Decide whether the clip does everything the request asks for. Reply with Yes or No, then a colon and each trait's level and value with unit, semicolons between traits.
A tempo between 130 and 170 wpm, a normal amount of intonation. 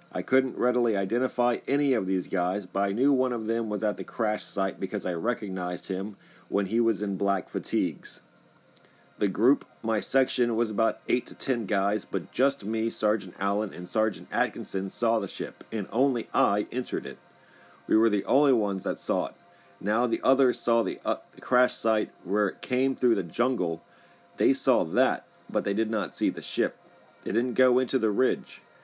No: average, 195 wpm; average, 3.9 semitones